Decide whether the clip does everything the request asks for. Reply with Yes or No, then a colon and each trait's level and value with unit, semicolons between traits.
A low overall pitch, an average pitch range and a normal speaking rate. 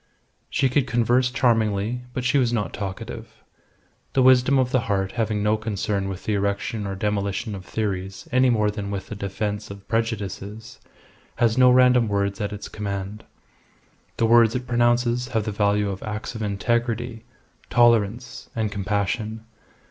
Yes: low, 110 Hz; average, 3.0 semitones; average, 160 wpm